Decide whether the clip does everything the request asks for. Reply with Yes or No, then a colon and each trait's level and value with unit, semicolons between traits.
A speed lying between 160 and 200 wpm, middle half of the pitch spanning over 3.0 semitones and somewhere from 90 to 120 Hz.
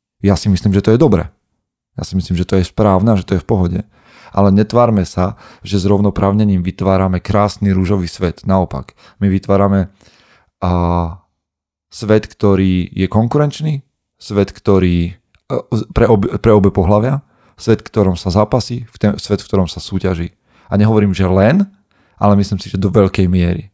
No: fast, 165 wpm; narrow, 2.4 semitones; low, 100 Hz